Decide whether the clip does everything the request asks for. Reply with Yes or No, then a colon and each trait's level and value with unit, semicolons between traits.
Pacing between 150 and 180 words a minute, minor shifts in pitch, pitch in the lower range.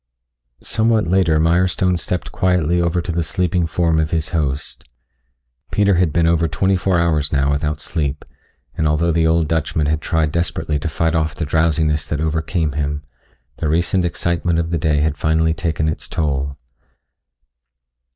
Yes: average, 165 wpm; narrow, 2.0 semitones; very low, 80 Hz